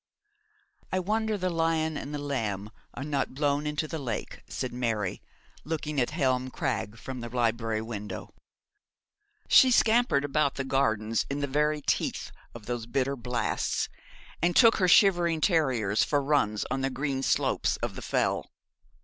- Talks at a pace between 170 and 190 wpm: No, average, 160 wpm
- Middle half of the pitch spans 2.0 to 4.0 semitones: No, average, 4.7 semitones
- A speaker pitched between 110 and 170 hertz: Yes, medium, 140 Hz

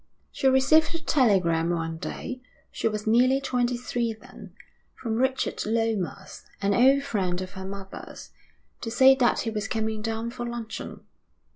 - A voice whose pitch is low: No, high, 225 Hz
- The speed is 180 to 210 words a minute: No, average, 155 wpm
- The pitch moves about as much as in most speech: Yes, average, 4.3 semitones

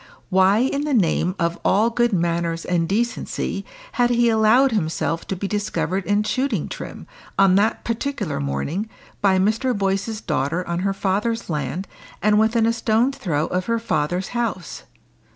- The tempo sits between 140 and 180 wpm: Yes, average, 160 wpm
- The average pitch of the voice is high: Yes, high, 200 Hz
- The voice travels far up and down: No, average, 4.6 semitones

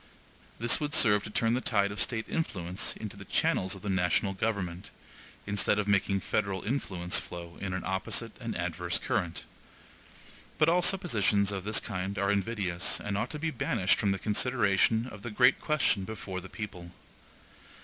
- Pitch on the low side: Yes, low, 100 Hz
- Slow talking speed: No, average, 175 wpm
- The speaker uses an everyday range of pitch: Yes, average, 3.1 semitones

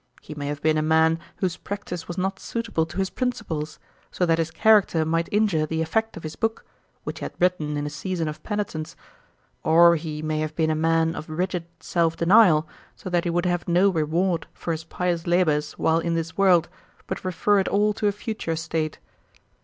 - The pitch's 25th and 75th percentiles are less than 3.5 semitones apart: Yes, average, 2.8 semitones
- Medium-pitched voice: Yes, medium, 165 Hz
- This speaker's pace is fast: Yes, fast, 210 wpm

